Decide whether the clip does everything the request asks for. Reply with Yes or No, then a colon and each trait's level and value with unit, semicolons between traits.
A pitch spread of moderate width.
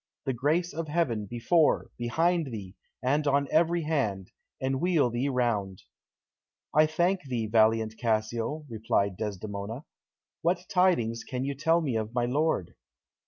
No: wide, 6.0 semitones